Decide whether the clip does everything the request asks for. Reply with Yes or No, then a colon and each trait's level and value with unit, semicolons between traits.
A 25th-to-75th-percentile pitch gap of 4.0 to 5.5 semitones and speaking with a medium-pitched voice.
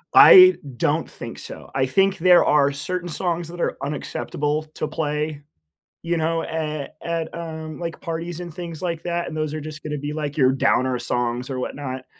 No: average, 2.7 semitones; medium, 155 Hz